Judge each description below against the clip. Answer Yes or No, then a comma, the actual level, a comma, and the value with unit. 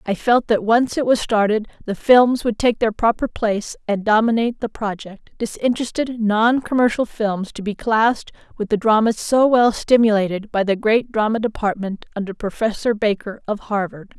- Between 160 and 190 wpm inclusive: Yes, average, 170 wpm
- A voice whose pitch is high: Yes, high, 220 Hz